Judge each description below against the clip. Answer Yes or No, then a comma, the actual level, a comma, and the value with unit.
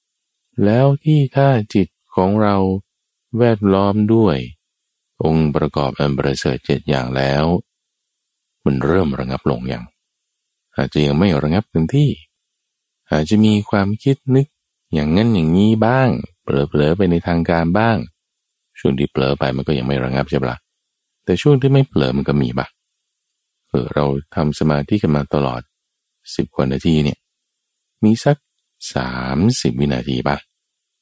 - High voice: No, very low, 80 Hz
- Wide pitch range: Yes, wide, 7.2 semitones